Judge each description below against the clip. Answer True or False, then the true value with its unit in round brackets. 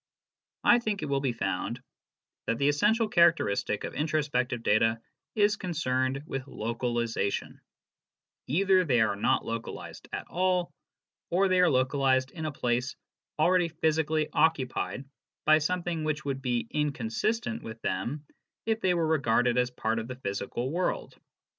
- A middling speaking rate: True (145 wpm)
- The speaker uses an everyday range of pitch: False (5.9 semitones)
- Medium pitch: True (145 Hz)